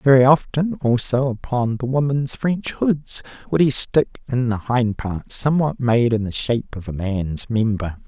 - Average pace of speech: Yes, average, 180 wpm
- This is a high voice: No, low, 125 Hz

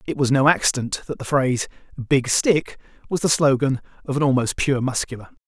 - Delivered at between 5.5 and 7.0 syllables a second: Yes, 5.6 syllables/s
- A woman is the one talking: No, male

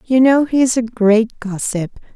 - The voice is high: Yes, high, 235 Hz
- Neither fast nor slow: Yes, average, 195 wpm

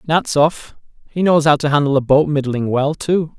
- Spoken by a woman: No, male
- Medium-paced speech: Yes, average, 195 wpm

